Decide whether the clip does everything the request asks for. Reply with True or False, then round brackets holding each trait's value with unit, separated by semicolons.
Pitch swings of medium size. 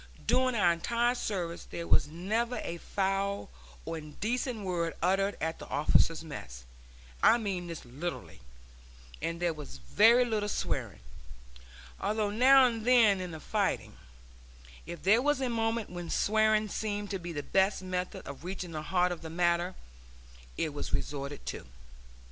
True (4.5 semitones)